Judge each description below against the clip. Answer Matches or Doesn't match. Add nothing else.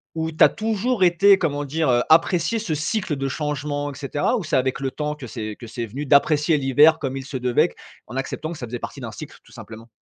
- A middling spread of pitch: Matches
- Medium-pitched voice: Matches